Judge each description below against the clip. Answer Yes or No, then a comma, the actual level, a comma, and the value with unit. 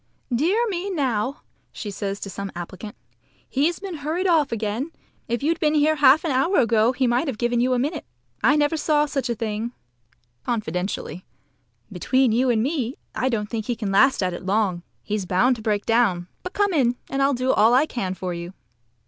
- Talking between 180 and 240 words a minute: Yes, average, 200 wpm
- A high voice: Yes, high, 245 Hz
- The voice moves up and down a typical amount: No, wide, 5.8 semitones